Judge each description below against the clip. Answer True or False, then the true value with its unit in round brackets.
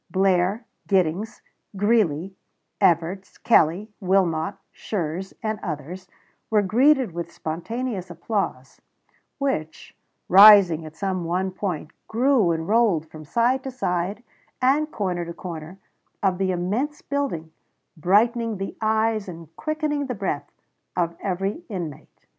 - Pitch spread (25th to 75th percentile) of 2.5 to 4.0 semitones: False (4.8 semitones)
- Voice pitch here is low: False (190 Hz)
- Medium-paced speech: False (120 wpm)